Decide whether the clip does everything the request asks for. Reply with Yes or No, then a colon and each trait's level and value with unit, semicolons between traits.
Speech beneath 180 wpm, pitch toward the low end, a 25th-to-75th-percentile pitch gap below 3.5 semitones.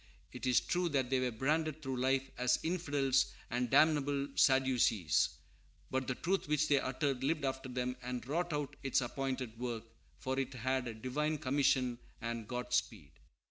Yes: average, 160 wpm; low, 130 Hz; narrow, 2.5 semitones